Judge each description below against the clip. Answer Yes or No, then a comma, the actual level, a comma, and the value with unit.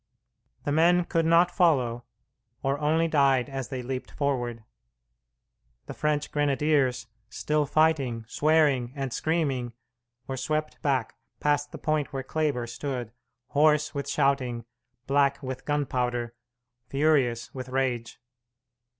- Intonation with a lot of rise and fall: No, average, 3.3 semitones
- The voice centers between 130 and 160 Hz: Yes, medium, 140 Hz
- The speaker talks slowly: Yes, slow, 120 wpm